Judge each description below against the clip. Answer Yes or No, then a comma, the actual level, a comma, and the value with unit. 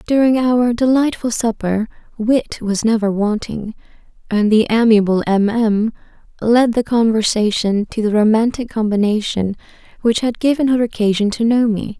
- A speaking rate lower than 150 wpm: Yes, average, 140 wpm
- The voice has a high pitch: Yes, high, 225 Hz